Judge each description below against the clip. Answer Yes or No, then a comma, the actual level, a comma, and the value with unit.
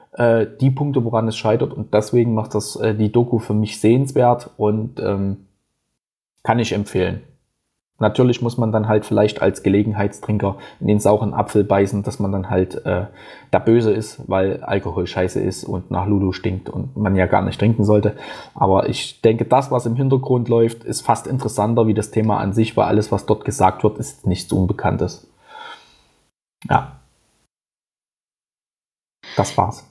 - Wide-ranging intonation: No, narrow, 2.5 semitones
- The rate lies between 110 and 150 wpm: No, average, 165 wpm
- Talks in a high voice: No, low, 110 Hz